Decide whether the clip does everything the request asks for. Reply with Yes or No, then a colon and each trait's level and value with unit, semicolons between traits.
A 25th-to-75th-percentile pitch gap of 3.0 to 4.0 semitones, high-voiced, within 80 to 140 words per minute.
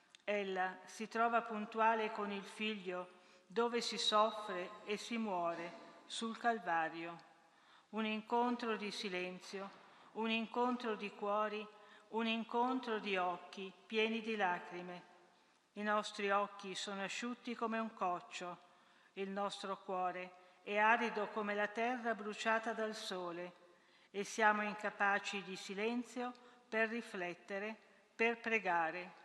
Yes: average, 3.5 semitones; high, 205 Hz; average, 120 wpm